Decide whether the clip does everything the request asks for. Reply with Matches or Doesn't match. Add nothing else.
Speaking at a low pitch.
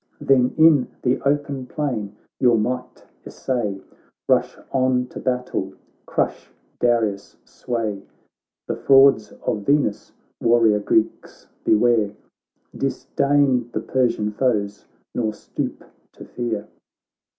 Matches